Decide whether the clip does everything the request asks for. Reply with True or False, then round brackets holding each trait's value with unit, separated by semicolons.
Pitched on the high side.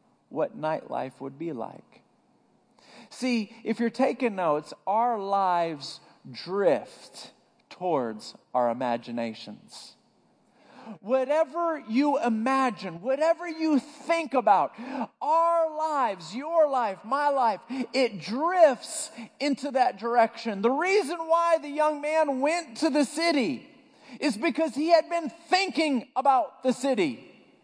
True (270 Hz)